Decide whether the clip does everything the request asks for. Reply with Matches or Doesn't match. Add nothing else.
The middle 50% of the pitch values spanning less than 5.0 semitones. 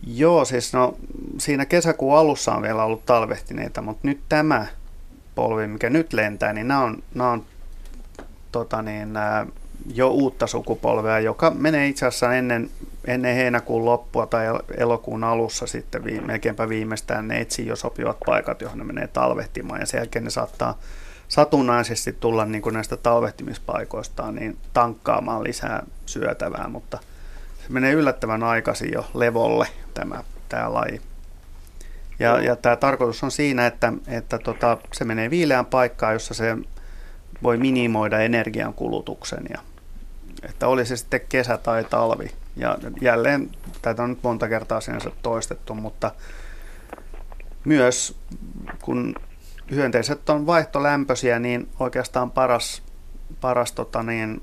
Matches